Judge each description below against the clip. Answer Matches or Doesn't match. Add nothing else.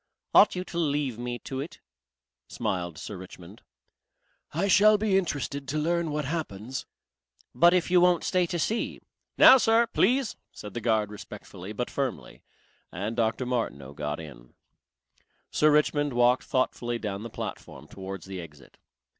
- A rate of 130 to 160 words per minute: Matches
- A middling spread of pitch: Doesn't match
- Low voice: Matches